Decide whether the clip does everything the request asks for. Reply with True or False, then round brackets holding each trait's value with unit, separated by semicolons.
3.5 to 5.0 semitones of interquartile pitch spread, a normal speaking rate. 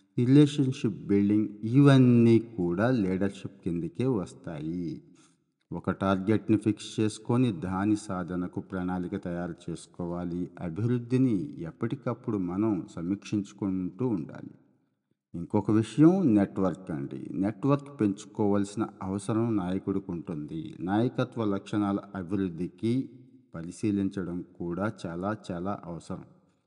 True (3.9 semitones; 85 wpm)